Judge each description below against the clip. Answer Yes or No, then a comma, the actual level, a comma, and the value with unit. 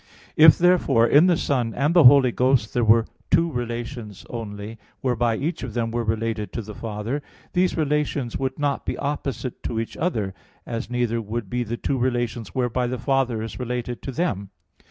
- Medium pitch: No, low, 120 Hz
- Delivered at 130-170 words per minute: No, average, 185 wpm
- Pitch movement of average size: Yes, average, 3.4 semitones